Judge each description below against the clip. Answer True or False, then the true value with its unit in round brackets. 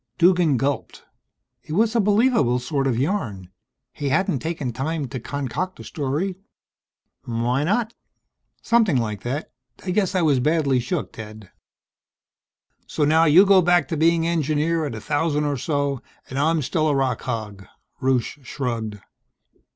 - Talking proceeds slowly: False (150 wpm)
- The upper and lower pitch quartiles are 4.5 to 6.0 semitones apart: True (5.0 semitones)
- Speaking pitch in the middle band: True (145 Hz)